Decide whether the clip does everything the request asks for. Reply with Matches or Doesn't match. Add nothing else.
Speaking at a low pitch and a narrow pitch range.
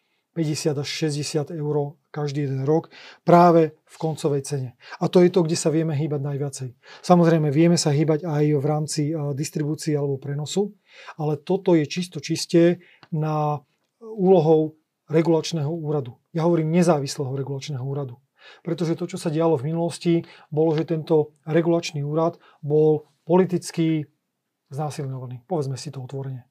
Doesn't match